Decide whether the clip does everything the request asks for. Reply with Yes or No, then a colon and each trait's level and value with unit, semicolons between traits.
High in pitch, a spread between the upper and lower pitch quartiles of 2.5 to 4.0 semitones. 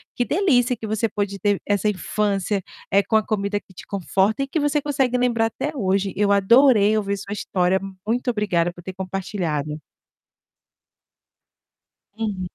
Yes: high, 205 Hz; average, 3.4 semitones